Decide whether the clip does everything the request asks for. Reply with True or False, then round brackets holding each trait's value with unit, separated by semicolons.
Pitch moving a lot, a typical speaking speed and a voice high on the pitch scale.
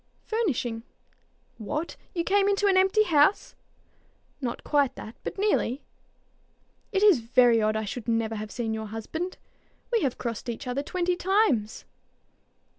True (8.9 semitones; 145 wpm; 275 Hz)